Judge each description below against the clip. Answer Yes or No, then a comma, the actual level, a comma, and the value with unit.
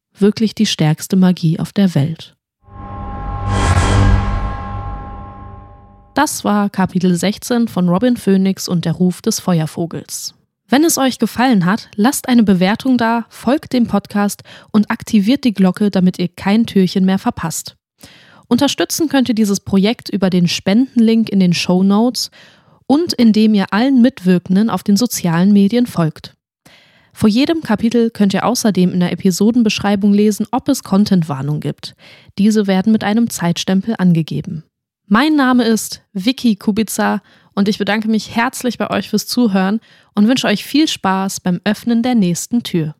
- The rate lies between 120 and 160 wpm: Yes, average, 150 wpm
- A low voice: No, high, 200 Hz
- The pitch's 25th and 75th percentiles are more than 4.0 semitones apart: Yes, average, 4.5 semitones